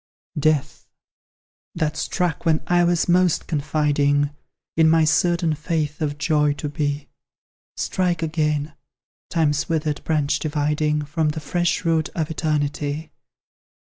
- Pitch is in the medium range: Yes, medium, 155 Hz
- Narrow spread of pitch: Yes, narrow, 1.8 semitones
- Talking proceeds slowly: Yes, slow, 120 wpm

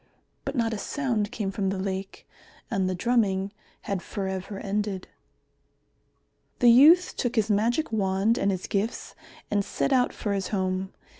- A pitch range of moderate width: Yes, average, 3.4 semitones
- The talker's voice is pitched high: Yes, high, 205 Hz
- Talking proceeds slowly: No, average, 160 wpm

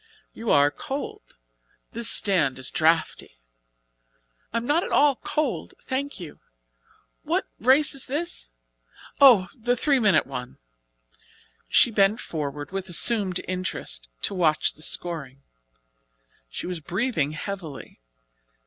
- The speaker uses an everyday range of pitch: No, wide, 8.2 semitones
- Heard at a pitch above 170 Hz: Yes, high, 190 Hz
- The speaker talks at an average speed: No, slow, 120 wpm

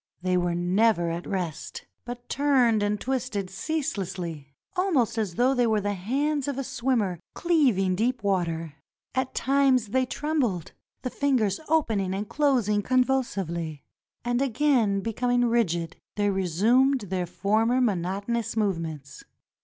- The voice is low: No, high, 220 Hz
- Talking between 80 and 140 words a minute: Yes, slow, 135 wpm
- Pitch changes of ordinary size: No, wide, 5.7 semitones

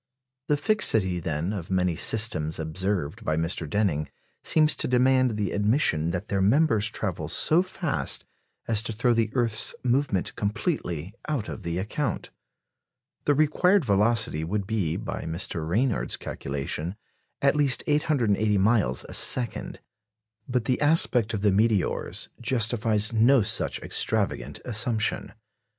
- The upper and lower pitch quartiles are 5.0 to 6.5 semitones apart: Yes, wide, 5.5 semitones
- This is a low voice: Yes, low, 110 Hz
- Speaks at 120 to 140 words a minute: Yes, slow, 135 wpm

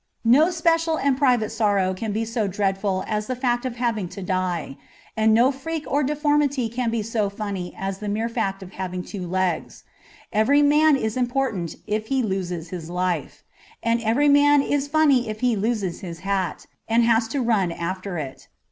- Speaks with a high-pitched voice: Yes, high, 220 Hz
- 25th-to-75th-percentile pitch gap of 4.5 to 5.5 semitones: Yes, average, 5.2 semitones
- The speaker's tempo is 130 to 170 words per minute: No, average, 185 wpm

